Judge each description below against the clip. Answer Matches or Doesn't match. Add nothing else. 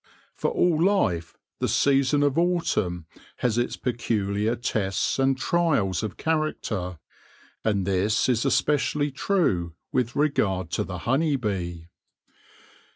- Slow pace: Matches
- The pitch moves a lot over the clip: Matches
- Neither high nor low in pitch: Doesn't match